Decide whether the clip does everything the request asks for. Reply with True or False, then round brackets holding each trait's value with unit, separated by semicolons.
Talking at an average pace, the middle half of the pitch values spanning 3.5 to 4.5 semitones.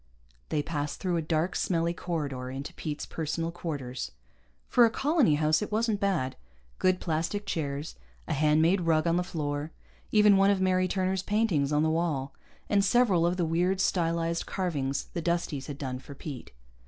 True (180 wpm; 4.0 semitones)